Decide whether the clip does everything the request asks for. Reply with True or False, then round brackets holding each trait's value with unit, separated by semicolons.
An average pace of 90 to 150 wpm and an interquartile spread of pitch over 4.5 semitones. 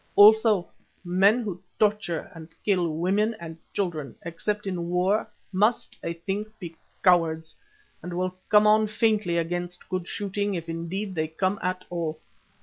False (145 wpm; 3.5 semitones)